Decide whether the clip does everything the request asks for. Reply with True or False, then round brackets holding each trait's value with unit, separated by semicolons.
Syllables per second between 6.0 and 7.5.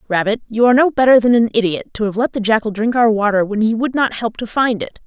True (6.3 syllables/s)